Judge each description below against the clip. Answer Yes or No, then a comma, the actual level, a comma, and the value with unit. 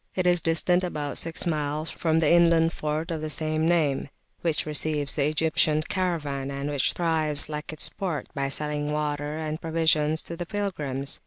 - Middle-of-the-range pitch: Yes, medium, 155 Hz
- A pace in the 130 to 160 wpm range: No, average, 175 wpm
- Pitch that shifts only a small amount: Yes, narrow, 1.9 semitones